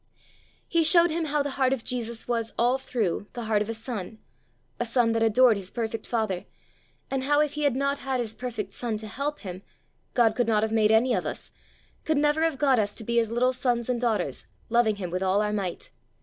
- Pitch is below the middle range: No, high, 235 Hz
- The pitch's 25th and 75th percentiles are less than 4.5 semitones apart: Yes, average, 3.4 semitones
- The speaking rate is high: Yes, fast, 230 wpm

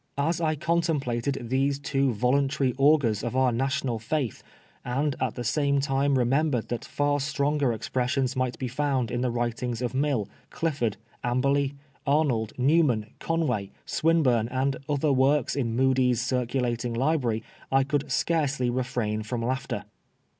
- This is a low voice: Yes, low, 130 Hz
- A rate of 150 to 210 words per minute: No, average, 140 wpm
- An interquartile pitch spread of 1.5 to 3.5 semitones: Yes, average, 2.8 semitones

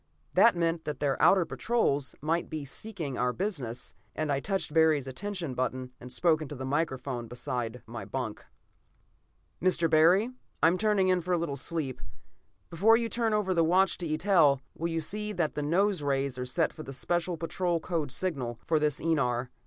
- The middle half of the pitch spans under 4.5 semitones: No, average, 5.1 semitones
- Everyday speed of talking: Yes, average, 185 wpm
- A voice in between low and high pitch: Yes, medium, 160 Hz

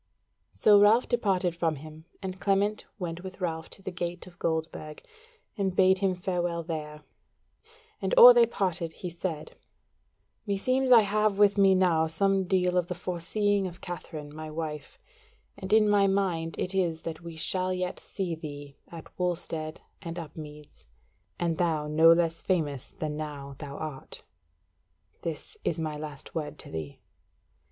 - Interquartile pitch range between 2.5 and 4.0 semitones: Yes, average, 3.4 semitones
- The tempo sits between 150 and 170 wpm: Yes, average, 160 wpm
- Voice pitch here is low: No, medium, 175 Hz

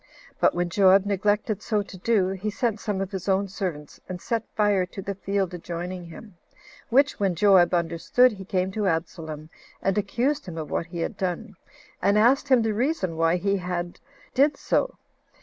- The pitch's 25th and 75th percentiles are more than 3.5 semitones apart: No, average, 3.2 semitones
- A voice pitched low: No, high, 195 Hz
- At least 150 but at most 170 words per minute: No, average, 185 wpm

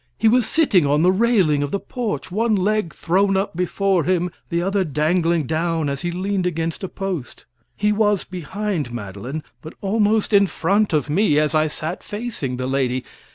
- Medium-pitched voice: Yes, medium, 180 Hz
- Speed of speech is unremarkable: Yes, average, 185 wpm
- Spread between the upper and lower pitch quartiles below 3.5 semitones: No, average, 4.9 semitones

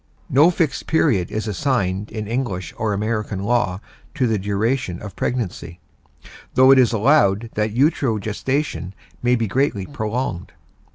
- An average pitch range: Yes, average, 4.6 semitones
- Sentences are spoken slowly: No, average, 145 wpm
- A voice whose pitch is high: No, low, 110 Hz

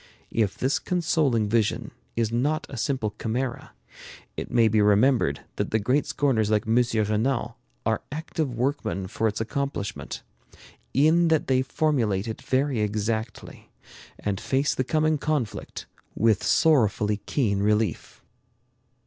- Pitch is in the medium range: No, low, 115 Hz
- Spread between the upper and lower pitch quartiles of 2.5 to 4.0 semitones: No, average, 4.5 semitones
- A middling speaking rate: No, slow, 130 wpm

